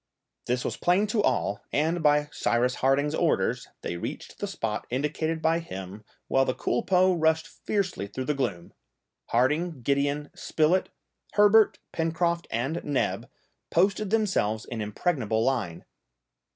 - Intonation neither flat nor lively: No, wide, 5.8 semitones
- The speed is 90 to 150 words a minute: Yes, slow, 135 wpm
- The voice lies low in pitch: No, medium, 150 Hz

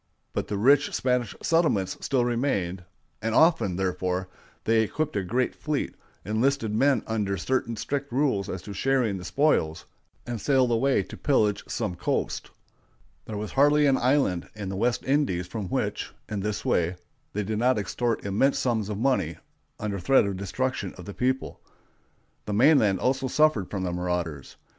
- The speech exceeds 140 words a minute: Yes, average, 165 wpm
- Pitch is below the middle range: Yes, low, 110 Hz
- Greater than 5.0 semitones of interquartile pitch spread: Yes, wide, 5.6 semitones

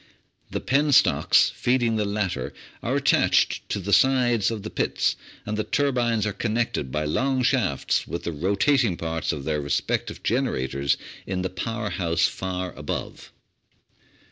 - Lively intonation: Yes, wide, 6.1 semitones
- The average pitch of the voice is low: Yes, low, 105 Hz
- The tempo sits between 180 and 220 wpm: No, average, 150 wpm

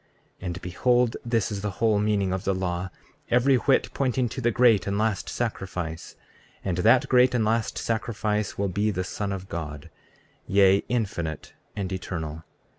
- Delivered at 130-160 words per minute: No, average, 170 wpm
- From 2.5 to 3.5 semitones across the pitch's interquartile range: No, average, 4.0 semitones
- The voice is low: Yes, low, 100 Hz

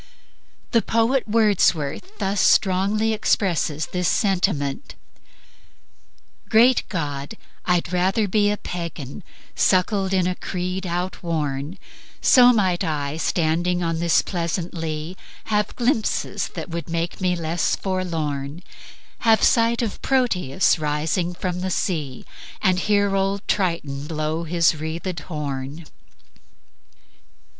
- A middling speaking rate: No, slow, 115 wpm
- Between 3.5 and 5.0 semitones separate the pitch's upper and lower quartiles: Yes, average, 4.0 semitones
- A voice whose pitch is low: No, medium, 180 Hz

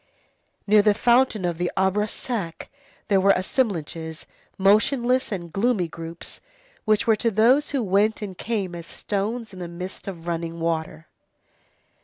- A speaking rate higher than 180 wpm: No, average, 150 wpm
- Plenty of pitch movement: No, average, 4.4 semitones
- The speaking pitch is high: Yes, high, 195 Hz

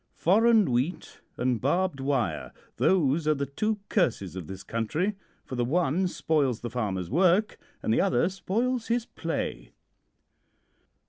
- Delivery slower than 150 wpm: Yes, average, 140 wpm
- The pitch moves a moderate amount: No, wide, 7.7 semitones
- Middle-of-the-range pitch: Yes, medium, 150 Hz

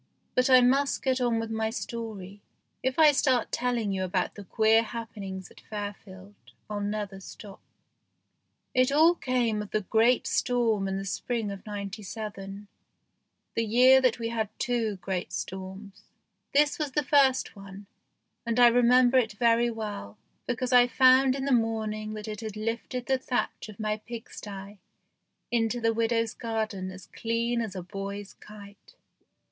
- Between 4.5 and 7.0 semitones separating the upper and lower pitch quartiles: No, average, 3.3 semitones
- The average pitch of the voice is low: No, high, 225 Hz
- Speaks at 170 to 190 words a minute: No, average, 160 wpm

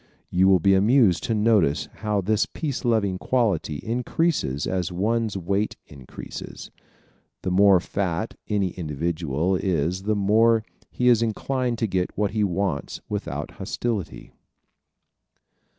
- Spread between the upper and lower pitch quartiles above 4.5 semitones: No, average, 3.9 semitones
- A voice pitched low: Yes, low, 100 Hz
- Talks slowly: Yes, slow, 130 wpm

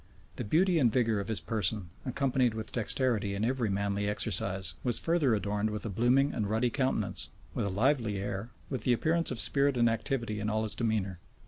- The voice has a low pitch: Yes, low, 110 Hz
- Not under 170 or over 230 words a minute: Yes, average, 200 wpm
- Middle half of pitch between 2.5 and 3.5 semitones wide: No, average, 3.9 semitones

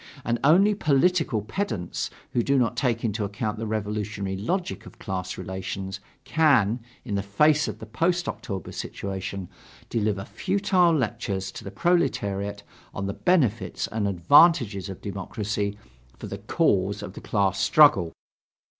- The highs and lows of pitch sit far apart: Yes, wide, 6.7 semitones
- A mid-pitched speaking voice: No, low, 105 Hz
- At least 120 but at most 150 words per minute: Yes, average, 145 wpm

